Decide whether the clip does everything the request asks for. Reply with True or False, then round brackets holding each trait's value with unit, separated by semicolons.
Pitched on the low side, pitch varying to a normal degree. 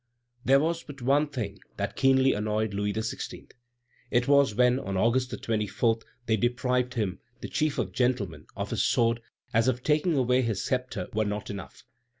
True (120 Hz; 3.8 semitones)